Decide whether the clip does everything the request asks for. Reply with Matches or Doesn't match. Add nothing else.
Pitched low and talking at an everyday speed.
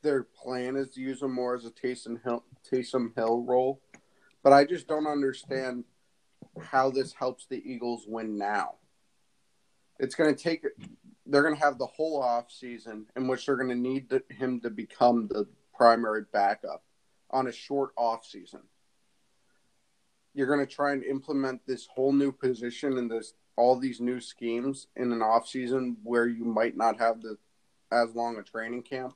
Matches